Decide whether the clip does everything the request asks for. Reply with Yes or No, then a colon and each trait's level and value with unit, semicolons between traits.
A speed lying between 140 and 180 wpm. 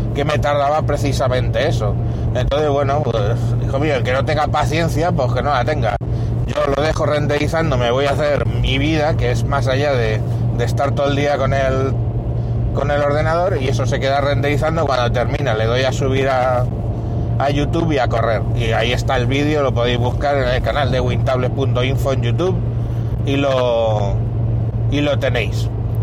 No: fast, 190 wpm